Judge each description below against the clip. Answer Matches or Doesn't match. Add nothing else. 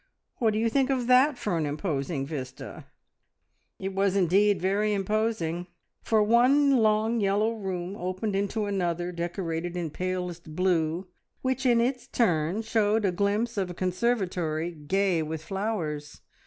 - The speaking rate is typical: Matches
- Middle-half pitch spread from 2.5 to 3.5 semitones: Doesn't match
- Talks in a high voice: Matches